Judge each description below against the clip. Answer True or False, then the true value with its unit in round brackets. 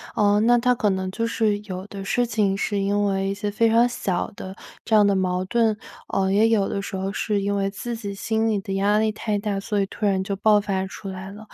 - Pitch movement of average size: False (2.0 semitones)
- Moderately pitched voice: False (205 Hz)